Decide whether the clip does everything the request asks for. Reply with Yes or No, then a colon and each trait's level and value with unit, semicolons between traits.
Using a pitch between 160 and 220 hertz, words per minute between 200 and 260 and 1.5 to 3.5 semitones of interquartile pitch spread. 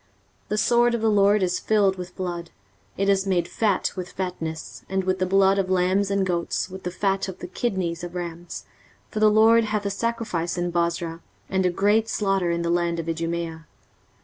Yes: medium, 185 Hz; fast, 205 wpm; narrow, 2.6 semitones